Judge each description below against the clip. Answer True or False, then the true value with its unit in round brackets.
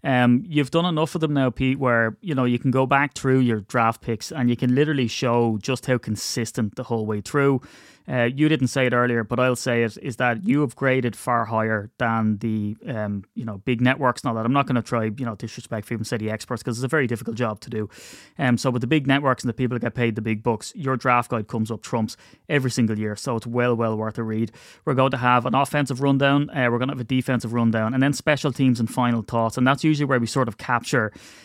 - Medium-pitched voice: False (125 Hz)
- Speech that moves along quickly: True (265 wpm)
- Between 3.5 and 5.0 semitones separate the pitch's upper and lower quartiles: False (2.5 semitones)